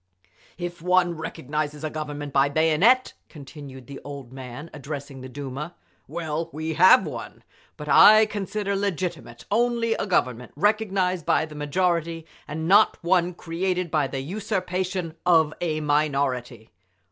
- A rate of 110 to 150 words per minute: Yes, slow, 135 wpm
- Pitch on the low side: No, medium, 160 Hz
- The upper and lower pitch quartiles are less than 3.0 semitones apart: No, average, 4.2 semitones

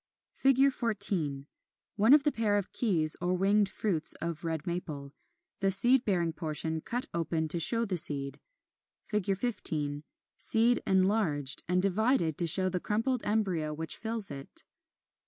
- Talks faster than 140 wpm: Yes, average, 150 wpm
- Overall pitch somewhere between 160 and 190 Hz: Yes, medium, 185 Hz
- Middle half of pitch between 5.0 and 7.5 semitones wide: Yes, wide, 5.4 semitones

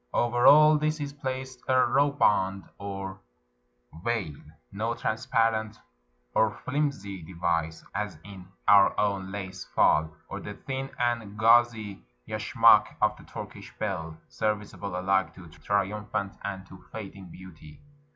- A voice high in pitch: No, low, 100 Hz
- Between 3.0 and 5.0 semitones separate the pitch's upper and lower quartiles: Yes, average, 4.0 semitones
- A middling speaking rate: No, slow, 130 wpm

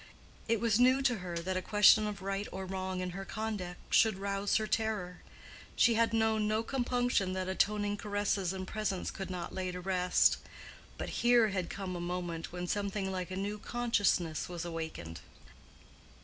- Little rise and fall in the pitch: No, average, 3.0 semitones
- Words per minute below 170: No, average, 175 wpm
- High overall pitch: Yes, high, 195 Hz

